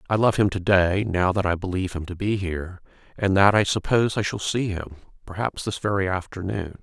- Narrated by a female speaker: No, male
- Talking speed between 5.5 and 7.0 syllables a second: Yes, 5.8 syllables/s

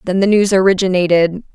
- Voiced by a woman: Yes, female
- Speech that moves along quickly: No, average, 155 wpm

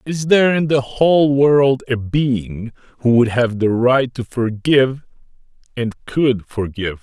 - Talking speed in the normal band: Yes, average, 155 wpm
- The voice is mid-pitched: No, low, 125 Hz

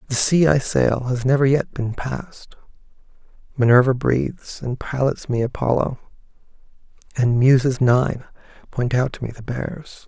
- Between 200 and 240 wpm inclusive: No, average, 145 wpm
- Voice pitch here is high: No, low, 130 Hz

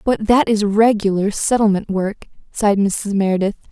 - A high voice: Yes, high, 205 Hz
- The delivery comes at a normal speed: Yes, average, 145 wpm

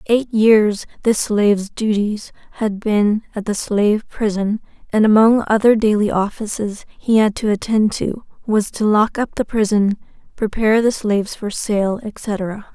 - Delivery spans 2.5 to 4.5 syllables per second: Yes, 4.3 syllables/s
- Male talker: No, female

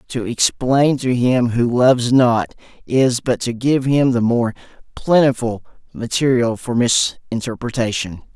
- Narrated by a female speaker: No, male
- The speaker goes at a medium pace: No, slow, 130 wpm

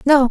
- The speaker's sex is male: No, female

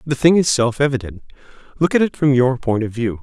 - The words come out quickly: Yes, fast, 240 wpm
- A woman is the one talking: No, male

